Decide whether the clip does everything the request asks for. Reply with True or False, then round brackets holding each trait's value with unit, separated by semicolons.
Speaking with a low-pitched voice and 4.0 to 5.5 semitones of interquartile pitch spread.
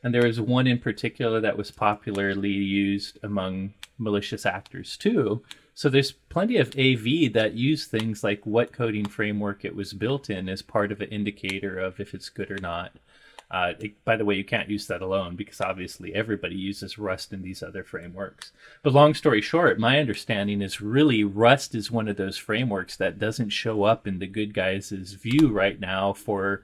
False (105 Hz; 3.0 semitones)